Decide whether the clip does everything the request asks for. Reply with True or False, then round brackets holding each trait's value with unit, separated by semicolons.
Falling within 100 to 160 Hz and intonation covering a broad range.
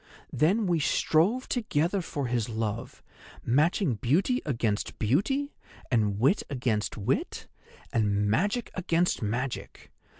True (140 Hz; 8.6 semitones)